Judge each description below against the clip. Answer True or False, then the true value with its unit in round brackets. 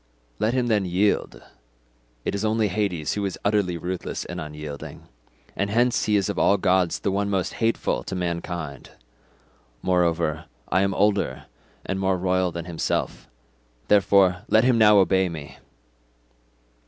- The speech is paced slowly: False (145 wpm)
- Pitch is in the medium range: False (95 Hz)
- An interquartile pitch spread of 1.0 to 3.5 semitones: True (3.0 semitones)